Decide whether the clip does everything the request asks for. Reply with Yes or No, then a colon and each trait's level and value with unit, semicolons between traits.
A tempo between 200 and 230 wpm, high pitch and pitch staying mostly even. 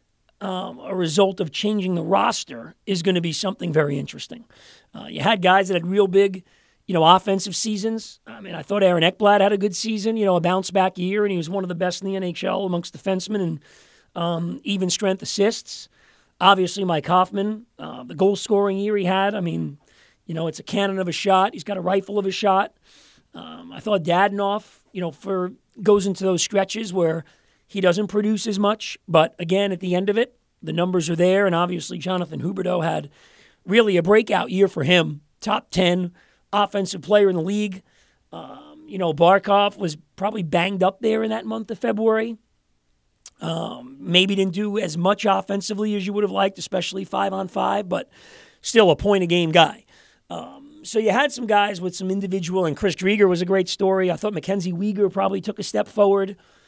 Yes: fast, 205 wpm; high, 195 Hz; narrow, 2.3 semitones